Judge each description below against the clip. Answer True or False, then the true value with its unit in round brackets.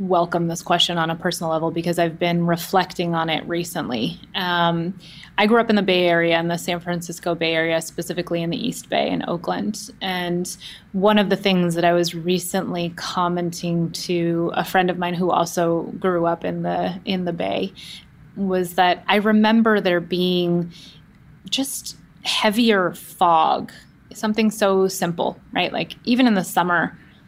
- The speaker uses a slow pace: False (170 wpm)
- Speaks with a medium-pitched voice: True (175 Hz)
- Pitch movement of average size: False (2.0 semitones)